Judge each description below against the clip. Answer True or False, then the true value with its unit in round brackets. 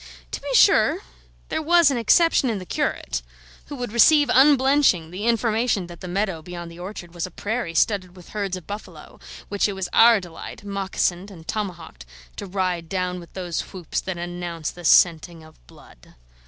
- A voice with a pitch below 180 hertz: False (185 Hz)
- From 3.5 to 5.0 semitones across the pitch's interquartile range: True (4.0 semitones)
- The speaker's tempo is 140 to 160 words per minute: False (180 wpm)